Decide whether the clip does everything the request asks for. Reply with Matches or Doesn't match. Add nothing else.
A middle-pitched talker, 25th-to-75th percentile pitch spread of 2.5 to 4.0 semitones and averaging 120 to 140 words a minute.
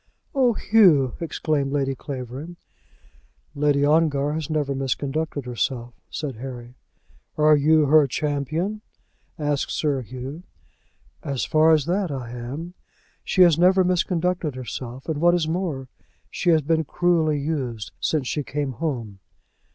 Matches